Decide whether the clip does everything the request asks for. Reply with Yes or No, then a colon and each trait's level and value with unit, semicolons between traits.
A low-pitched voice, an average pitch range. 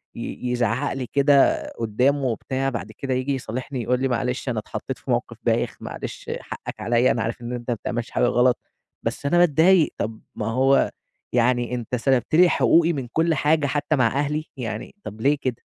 Yes: low, 130 Hz; average, 3.0 semitones